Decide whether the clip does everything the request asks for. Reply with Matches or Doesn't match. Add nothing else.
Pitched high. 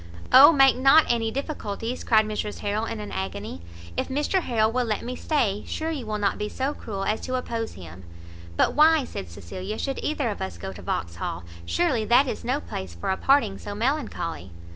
Matches